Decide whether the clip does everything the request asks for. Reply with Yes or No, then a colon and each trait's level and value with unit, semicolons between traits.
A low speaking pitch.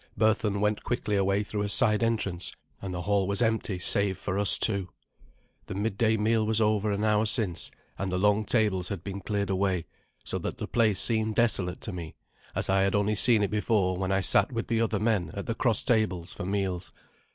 Yes: low, 105 Hz